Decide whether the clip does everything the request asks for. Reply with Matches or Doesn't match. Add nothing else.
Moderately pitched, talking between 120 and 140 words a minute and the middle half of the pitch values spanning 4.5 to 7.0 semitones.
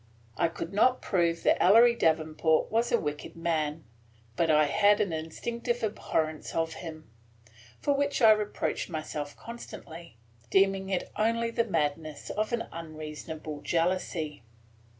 Matches